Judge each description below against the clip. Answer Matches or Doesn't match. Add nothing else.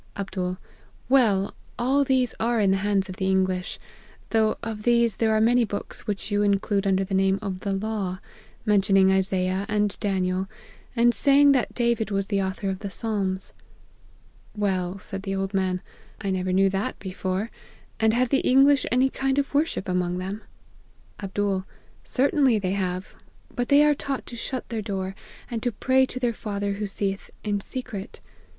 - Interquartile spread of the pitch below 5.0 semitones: Matches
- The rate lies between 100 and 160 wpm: Doesn't match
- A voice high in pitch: Matches